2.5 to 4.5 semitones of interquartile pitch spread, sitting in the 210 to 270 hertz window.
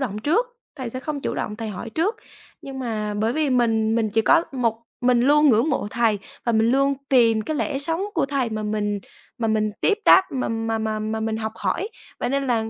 Yes: average, 4.0 semitones; high, 235 Hz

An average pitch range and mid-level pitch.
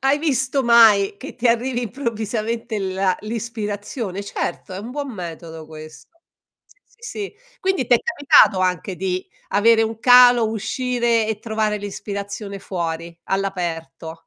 No: average, 4.1 semitones; high, 215 Hz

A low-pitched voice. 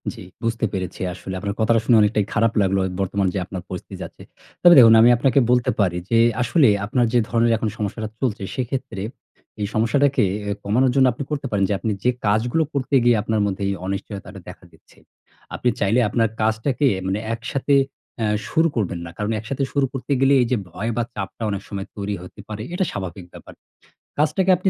Yes: low, 115 Hz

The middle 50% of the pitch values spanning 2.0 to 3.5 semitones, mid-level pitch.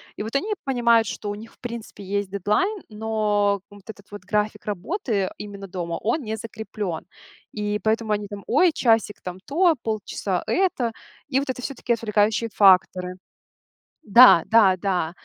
No: narrow, 2.6 semitones; high, 210 Hz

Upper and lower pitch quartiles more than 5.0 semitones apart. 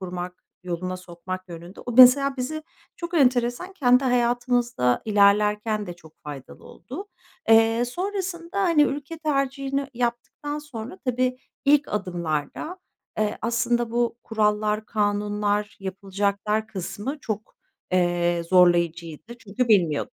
Yes: wide, 5.5 semitones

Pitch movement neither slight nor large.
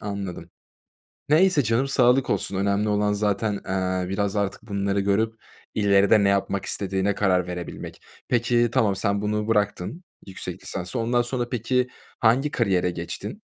Yes: average, 3.2 semitones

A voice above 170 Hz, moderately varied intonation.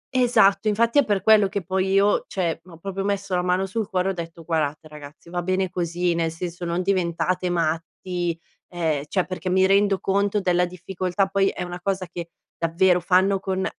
No: medium, 185 Hz; narrow, 2.3 semitones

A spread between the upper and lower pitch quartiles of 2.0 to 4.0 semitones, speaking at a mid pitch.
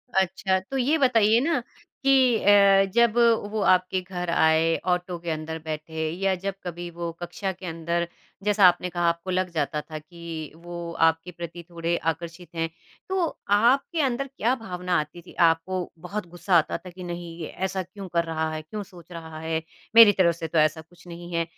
Yes: average, 2.9 semitones; medium, 175 Hz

